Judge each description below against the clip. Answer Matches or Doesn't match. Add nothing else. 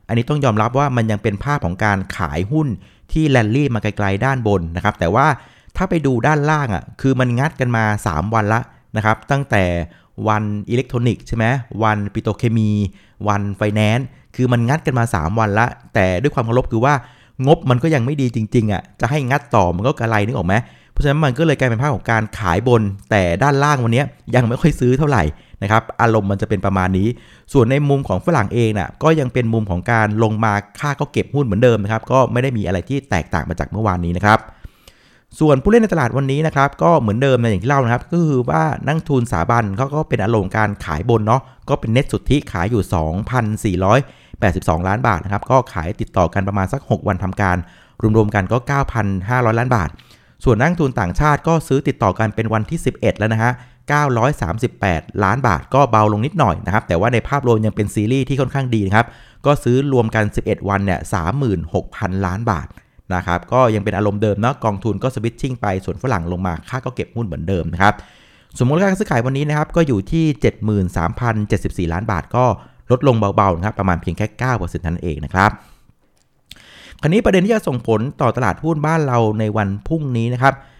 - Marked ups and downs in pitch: Doesn't match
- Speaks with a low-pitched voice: Matches